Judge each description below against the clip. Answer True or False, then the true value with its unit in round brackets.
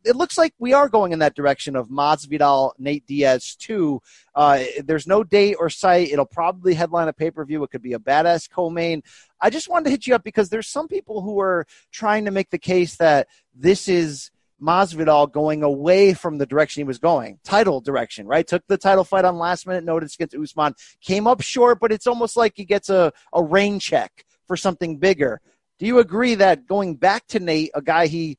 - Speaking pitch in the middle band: True (175 Hz)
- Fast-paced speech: True (215 wpm)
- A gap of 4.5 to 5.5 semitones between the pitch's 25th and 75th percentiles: True (4.9 semitones)